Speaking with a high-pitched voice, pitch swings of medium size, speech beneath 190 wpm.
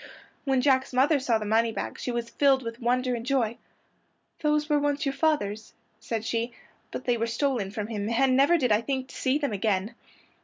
No: very high, 250 Hz; average, 3.3 semitones; average, 200 wpm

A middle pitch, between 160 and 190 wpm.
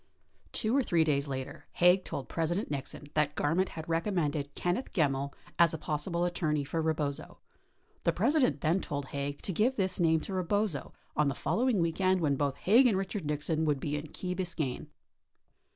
Yes: medium, 160 Hz; average, 185 wpm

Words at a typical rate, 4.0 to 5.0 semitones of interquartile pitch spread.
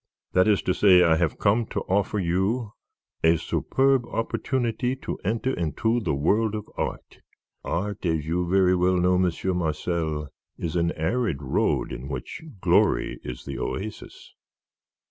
Yes: average, 150 wpm; average, 4.7 semitones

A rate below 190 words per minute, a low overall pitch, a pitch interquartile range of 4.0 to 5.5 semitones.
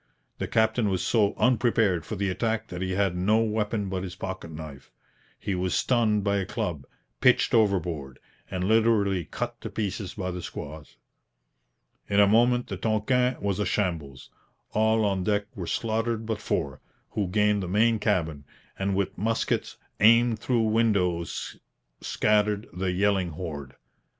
No: average, 155 wpm; low, 100 Hz; average, 3.4 semitones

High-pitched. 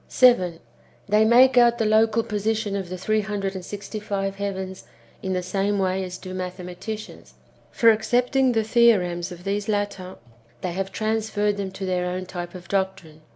Yes: high, 200 Hz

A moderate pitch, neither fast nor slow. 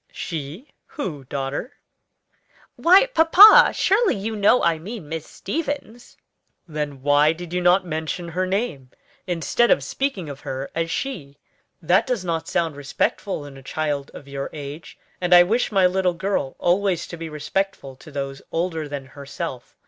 Yes: medium, 170 Hz; average, 160 wpm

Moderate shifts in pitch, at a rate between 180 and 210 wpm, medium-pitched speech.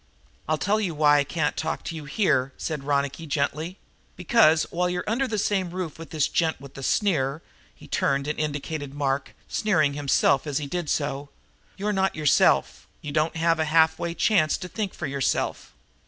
Yes: average, 3.9 semitones; average, 190 wpm; medium, 155 Hz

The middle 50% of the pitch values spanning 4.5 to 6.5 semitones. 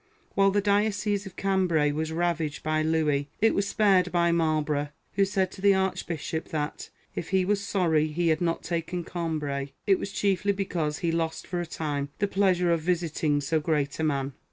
No: average, 3.7 semitones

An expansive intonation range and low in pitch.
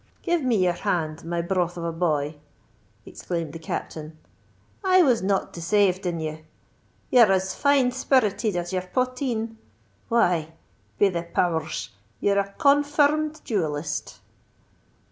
No: wide, 6.8 semitones; medium, 185 Hz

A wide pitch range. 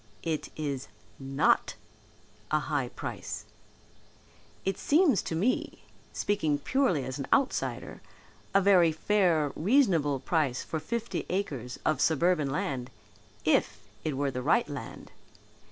Yes: wide, 6.1 semitones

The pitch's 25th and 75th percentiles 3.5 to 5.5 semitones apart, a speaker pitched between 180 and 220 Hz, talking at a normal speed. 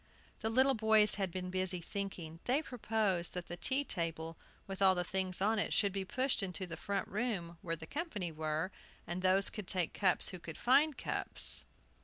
Yes: average, 3.9 semitones; high, 190 Hz; average, 190 wpm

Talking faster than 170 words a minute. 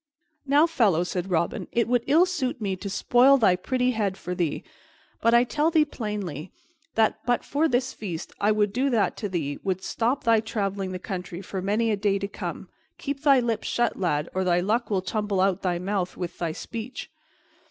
Yes: fast, 205 wpm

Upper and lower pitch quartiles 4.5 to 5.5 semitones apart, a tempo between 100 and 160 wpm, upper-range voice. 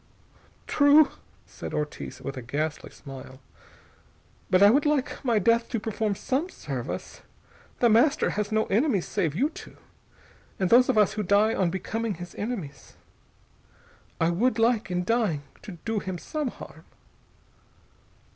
Yes: average, 5.1 semitones; average, 145 wpm; high, 215 Hz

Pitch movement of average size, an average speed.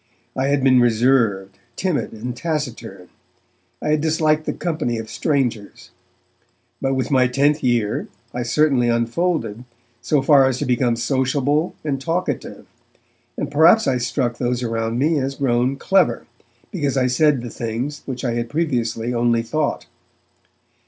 Yes: average, 3.8 semitones; average, 145 wpm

